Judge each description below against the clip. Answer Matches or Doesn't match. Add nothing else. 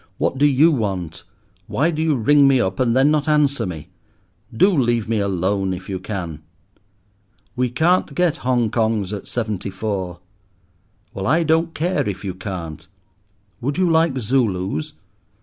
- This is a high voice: Doesn't match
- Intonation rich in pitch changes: Matches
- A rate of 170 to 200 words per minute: Doesn't match